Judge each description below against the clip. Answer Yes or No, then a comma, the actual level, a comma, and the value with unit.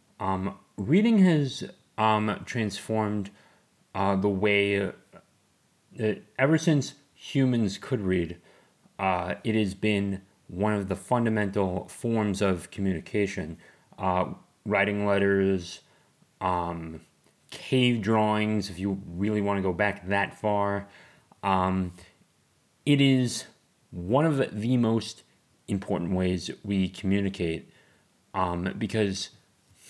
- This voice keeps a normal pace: No, slow, 105 wpm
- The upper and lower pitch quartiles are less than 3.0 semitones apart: Yes, narrow, 2.6 semitones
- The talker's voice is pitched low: Yes, low, 100 Hz